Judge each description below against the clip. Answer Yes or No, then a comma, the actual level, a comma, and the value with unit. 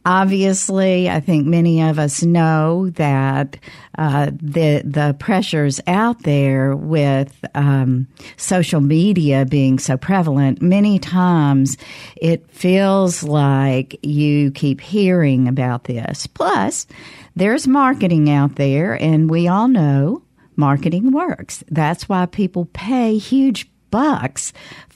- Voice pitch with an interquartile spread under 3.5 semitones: No, average, 4.7 semitones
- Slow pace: Yes, slow, 120 wpm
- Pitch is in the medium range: Yes, medium, 155 Hz